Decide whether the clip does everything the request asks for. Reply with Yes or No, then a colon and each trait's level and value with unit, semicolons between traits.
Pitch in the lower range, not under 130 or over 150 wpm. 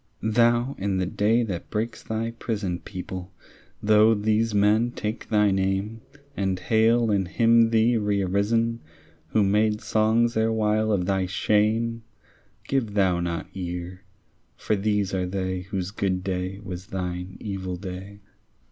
Yes: low, 105 Hz; average, 140 wpm